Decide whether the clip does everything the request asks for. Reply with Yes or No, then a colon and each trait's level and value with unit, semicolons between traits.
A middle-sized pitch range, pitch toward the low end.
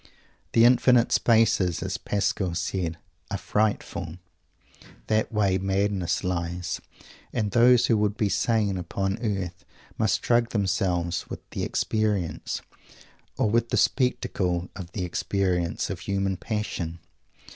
Yes: average, 3.5 semitones; low, 100 Hz